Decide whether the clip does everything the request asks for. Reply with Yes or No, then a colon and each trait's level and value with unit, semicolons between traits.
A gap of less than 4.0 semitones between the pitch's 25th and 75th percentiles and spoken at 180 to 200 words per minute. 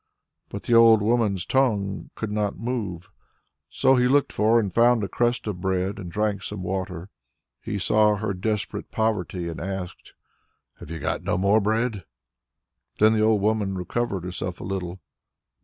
No: average, 2.9 semitones; average, 165 wpm